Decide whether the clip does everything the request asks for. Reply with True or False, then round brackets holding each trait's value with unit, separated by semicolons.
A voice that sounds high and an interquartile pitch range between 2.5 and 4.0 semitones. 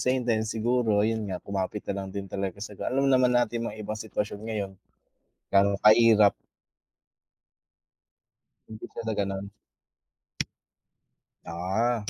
False (110 Hz; 2.8 semitones)